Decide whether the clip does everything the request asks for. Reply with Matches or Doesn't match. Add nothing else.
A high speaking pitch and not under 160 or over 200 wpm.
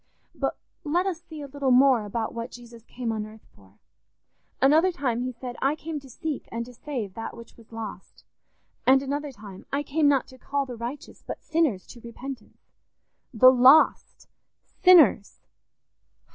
Matches